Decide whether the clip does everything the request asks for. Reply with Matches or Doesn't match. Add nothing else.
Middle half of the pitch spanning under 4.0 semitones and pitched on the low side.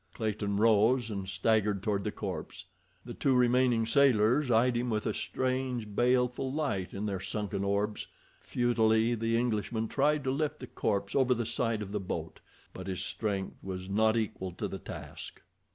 Matches